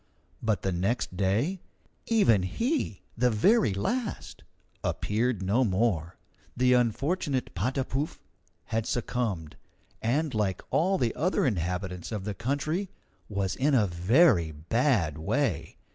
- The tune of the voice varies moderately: No, wide, 6.7 semitones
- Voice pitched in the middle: No, low, 115 Hz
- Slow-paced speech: Yes, slow, 120 wpm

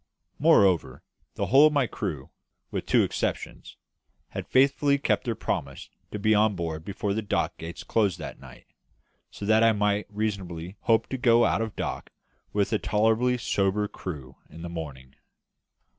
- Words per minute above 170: No, average, 165 wpm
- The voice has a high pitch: No, low, 105 Hz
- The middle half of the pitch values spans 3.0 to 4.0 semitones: No, average, 4.7 semitones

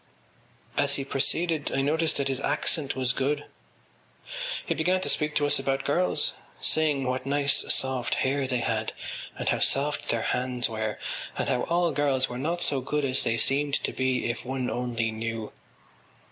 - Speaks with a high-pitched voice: No, low, 135 Hz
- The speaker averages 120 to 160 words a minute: No, average, 175 wpm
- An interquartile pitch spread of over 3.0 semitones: No, narrow, 2.6 semitones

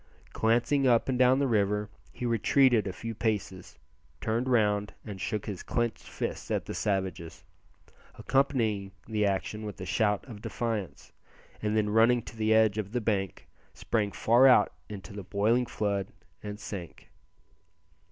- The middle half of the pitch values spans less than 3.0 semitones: Yes, narrow, 2.6 semitones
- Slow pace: No, average, 155 wpm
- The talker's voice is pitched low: Yes, low, 110 Hz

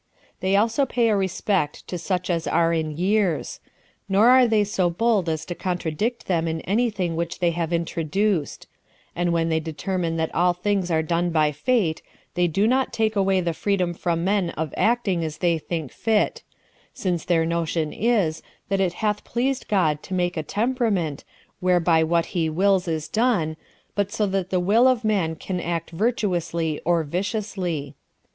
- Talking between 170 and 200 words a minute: Yes, average, 180 wpm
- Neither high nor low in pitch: Yes, medium, 180 Hz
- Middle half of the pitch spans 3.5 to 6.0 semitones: Yes, average, 3.9 semitones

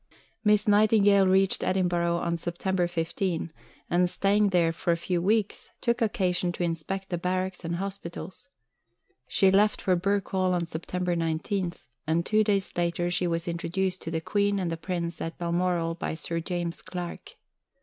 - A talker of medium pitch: Yes, medium, 180 Hz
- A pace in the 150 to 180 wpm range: Yes, average, 160 wpm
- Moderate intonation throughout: No, narrow, 2.3 semitones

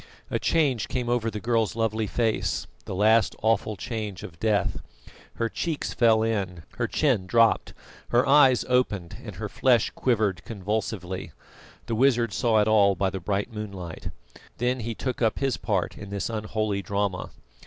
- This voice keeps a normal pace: Yes, average, 165 wpm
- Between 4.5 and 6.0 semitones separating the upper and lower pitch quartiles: No, average, 2.9 semitones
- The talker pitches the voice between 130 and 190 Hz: No, low, 110 Hz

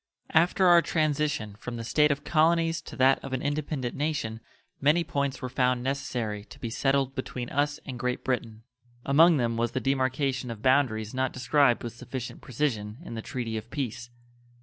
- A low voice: Yes, low, 130 Hz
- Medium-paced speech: Yes, average, 180 wpm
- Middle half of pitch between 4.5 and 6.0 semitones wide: No, average, 3.5 semitones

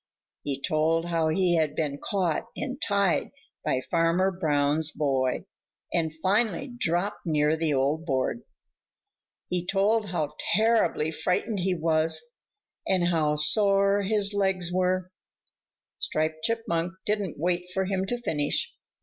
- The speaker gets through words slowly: Yes, slow, 130 wpm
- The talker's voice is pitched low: No, medium, 175 Hz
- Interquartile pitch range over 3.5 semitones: Yes, average, 3.9 semitones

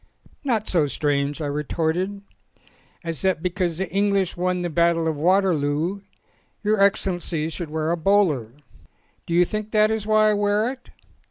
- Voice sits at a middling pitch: Yes, medium, 180 Hz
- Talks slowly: No, average, 165 wpm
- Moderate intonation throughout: Yes, average, 4.2 semitones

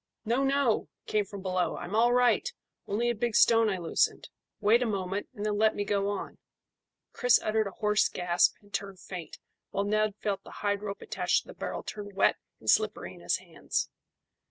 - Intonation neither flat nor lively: No, narrow, 2.1 semitones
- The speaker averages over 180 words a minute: Yes, average, 200 wpm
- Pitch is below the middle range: No, high, 210 Hz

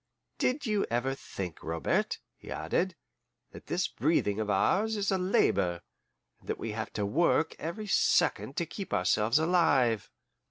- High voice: No, low, 135 Hz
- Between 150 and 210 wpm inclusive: Yes, average, 155 wpm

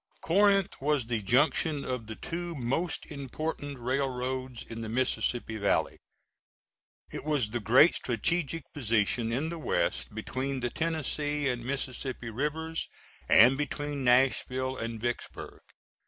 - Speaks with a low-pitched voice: Yes, low, 130 Hz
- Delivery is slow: Yes, slow, 125 wpm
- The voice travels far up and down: No, average, 3.7 semitones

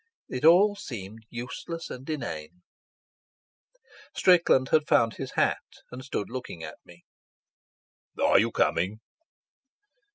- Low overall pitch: Yes, low, 125 Hz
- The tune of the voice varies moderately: No, wide, 8.0 semitones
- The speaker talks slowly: Yes, slow, 110 wpm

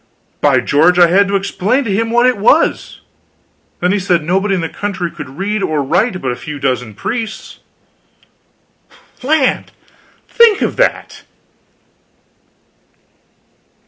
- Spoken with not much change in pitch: No, average, 5.3 semitones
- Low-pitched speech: No, high, 195 Hz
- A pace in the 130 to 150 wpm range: Yes, slow, 135 wpm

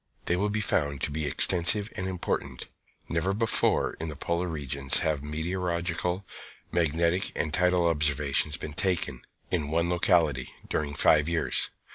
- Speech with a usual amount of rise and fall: Yes, average, 3.1 semitones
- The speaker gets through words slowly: No, average, 145 wpm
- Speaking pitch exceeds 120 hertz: No, very low, 85 Hz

